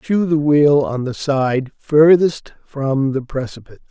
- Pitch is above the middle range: No, medium, 140 Hz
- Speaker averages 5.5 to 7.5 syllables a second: No, 4.0 syllables/s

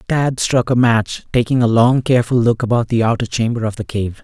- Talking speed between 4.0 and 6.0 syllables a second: Yes, 5.5 syllables/s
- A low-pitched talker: Yes, low, 120 Hz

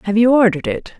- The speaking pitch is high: Yes, high, 215 Hz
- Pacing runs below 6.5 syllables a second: No, 7.5 syllables/s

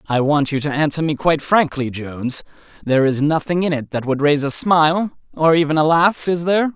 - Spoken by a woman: No, male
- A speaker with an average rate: No, fast, 215 wpm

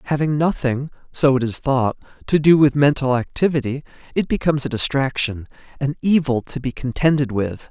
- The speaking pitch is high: No, medium, 140 Hz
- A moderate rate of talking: Yes, average, 165 wpm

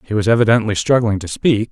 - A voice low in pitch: Yes, low, 110 Hz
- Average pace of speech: No, fast, 210 wpm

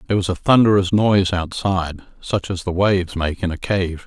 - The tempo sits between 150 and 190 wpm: No, fast, 205 wpm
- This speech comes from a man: Yes, male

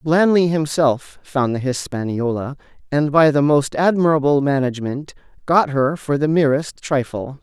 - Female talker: No, male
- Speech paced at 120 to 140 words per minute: Yes, slow, 135 wpm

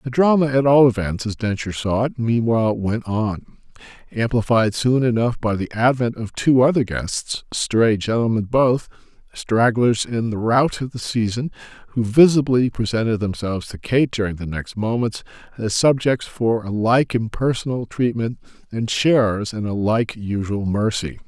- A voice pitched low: Yes, low, 115 Hz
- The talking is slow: No, average, 155 wpm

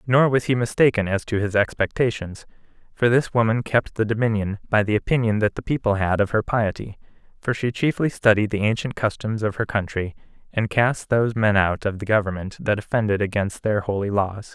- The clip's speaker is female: No, male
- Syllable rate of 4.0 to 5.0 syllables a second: No, 5.5 syllables/s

